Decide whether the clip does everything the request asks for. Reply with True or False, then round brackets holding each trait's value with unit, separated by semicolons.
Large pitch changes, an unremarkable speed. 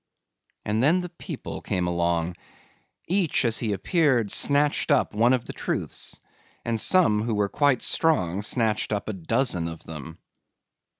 True (7.0 semitones; 155 wpm)